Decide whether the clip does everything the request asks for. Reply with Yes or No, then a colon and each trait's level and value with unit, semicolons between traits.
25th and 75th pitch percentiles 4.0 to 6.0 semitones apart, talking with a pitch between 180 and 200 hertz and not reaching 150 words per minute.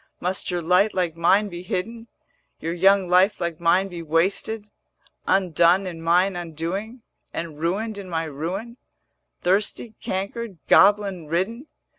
No: average, 3.2 semitones; medium, 185 Hz; average, 140 wpm